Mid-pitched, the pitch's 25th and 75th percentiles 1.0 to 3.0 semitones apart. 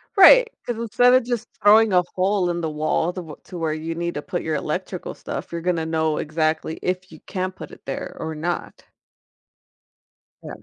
No: medium, 175 Hz; average, 4.0 semitones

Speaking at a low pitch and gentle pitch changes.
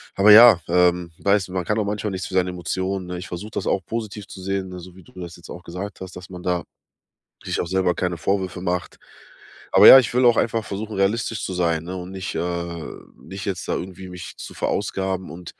Yes: very low, 95 Hz; narrow, 1.9 semitones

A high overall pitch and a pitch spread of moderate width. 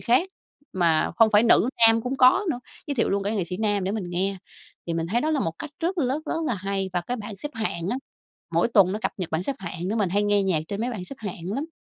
Yes: high, 205 Hz; average, 5.0 semitones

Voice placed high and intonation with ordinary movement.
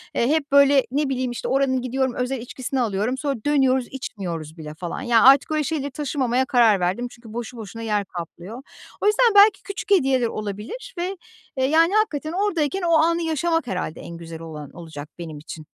No: very high, 260 Hz; wide, 6.7 semitones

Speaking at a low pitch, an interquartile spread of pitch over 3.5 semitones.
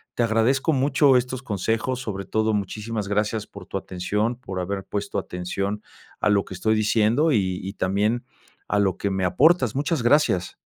Yes: low, 105 Hz; average, 3.9 semitones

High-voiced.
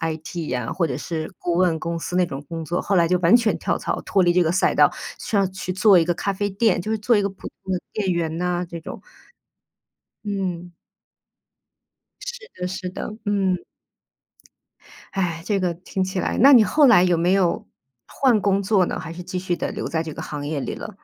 No: medium, 180 Hz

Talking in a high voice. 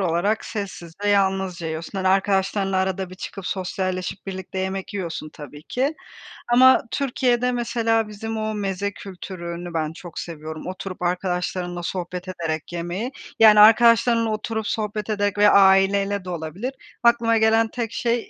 Yes: high, 195 Hz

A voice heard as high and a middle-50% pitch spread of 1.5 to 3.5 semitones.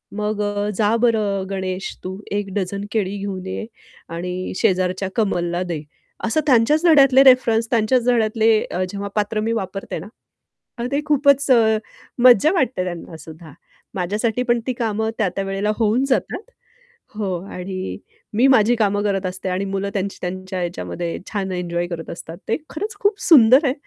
No: high, 205 Hz; average, 3.9 semitones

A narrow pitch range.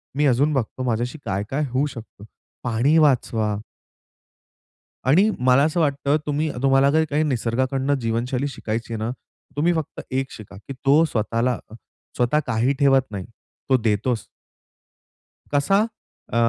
No: average, 3.7 semitones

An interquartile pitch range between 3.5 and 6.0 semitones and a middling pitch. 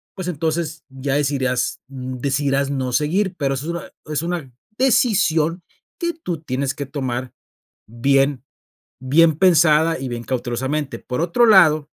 Yes: average, 4.1 semitones; medium, 145 Hz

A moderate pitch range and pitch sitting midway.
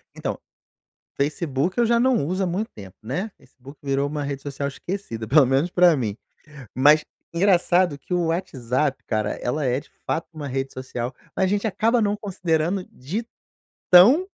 No: wide, 5.9 semitones; medium, 155 Hz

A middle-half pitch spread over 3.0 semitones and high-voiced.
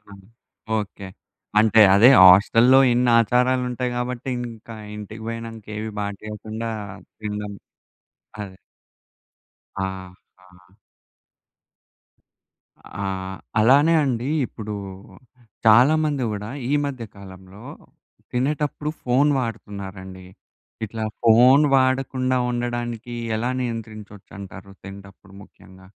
No: average, 3.7 semitones; low, 115 Hz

